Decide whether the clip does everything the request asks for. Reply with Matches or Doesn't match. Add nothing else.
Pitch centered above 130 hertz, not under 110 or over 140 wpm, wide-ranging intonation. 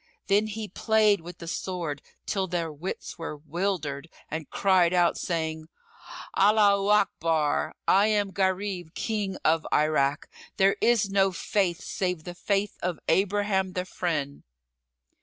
Doesn't match